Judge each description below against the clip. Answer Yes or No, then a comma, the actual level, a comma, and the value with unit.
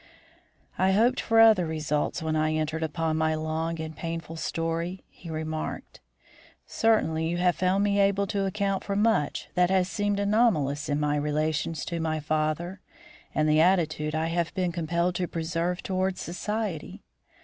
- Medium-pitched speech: Yes, medium, 165 Hz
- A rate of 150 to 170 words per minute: Yes, average, 160 wpm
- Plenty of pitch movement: No, average, 3.3 semitones